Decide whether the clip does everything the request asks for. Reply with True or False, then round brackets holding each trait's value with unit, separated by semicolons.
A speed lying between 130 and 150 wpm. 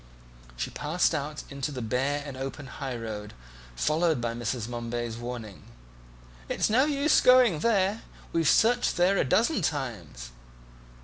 True (140 wpm)